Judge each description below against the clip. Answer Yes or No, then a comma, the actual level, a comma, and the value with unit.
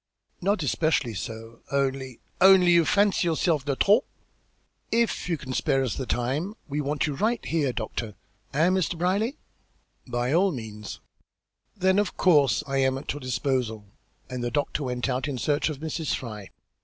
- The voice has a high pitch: No, medium, 140 Hz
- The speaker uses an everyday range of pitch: No, wide, 5.7 semitones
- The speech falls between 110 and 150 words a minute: No, average, 170 wpm